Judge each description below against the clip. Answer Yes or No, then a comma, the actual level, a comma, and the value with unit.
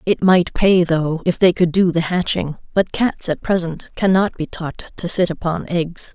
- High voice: No, medium, 175 Hz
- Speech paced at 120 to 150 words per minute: No, fast, 205 wpm